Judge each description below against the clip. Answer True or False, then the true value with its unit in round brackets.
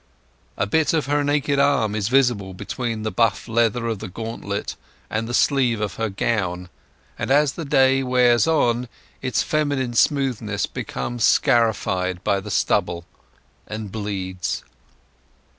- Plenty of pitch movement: False (4.7 semitones)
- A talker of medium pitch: False (115 Hz)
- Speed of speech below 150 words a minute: True (140 wpm)